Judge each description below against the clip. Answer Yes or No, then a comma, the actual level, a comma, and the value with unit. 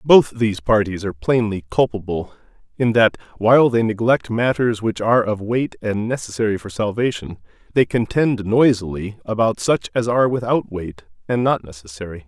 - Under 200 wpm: Yes, average, 155 wpm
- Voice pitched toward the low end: Yes, low, 110 Hz